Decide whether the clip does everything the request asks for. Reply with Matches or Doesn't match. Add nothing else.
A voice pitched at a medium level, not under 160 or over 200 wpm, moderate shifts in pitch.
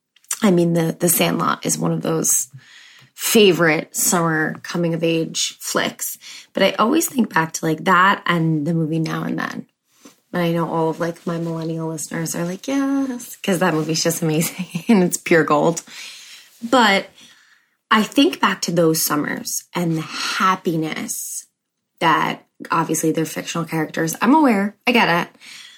Matches